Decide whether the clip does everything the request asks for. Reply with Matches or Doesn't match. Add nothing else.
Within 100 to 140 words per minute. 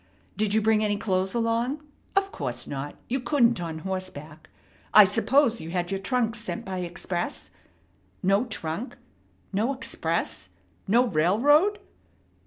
Matches